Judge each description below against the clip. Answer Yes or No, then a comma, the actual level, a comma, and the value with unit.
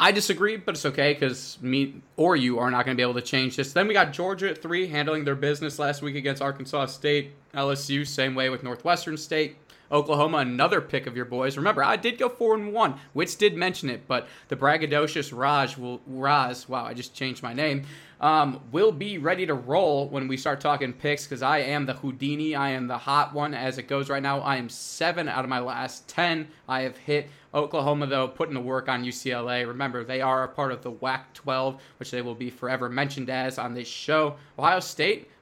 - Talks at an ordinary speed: No, fast, 225 wpm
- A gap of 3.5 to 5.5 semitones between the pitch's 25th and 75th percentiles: No, narrow, 2.5 semitones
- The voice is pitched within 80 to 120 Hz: No, medium, 140 Hz